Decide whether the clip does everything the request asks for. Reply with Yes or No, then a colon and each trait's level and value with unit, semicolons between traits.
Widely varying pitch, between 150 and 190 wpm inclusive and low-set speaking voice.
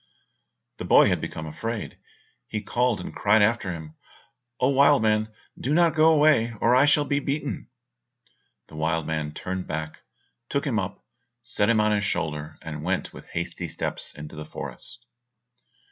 Yes: wide, 8.0 semitones; average, 165 wpm; low, 105 Hz